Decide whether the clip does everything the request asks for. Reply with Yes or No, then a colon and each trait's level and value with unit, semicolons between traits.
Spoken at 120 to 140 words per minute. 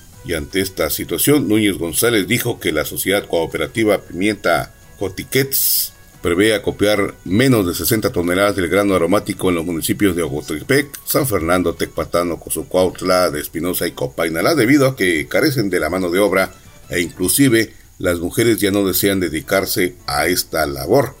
No: average, 155 wpm